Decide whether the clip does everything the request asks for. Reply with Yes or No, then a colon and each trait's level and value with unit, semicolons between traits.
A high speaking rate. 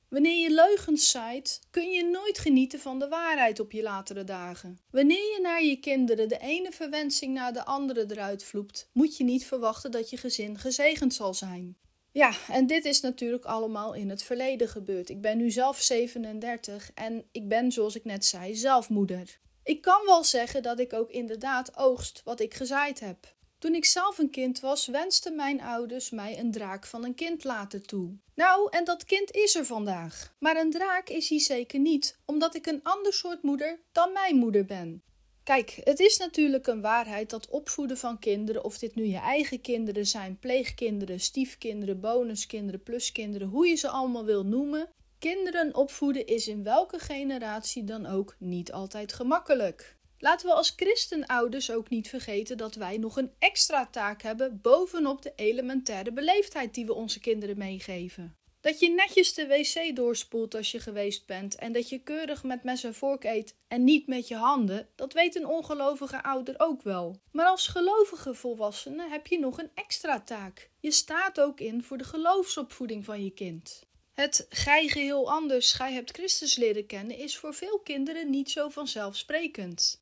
No: average, 180 wpm